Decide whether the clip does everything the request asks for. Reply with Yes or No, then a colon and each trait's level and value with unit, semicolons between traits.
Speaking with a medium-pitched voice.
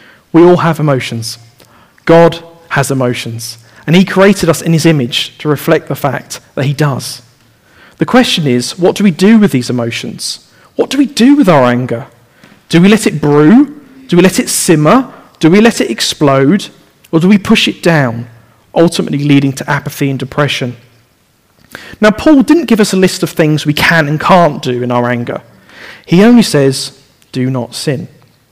Yes: medium, 150 Hz